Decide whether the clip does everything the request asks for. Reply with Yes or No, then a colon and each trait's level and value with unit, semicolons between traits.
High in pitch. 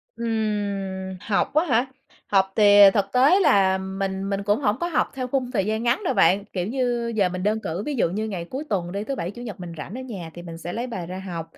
Yes: high, 205 Hz